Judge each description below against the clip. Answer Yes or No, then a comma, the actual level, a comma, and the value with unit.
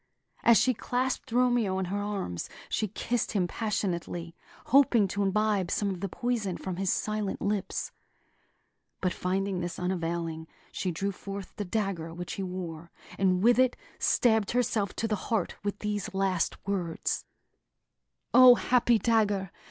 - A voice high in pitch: Yes, high, 200 Hz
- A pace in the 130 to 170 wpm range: Yes, average, 150 wpm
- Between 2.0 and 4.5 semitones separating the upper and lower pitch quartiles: Yes, average, 3.4 semitones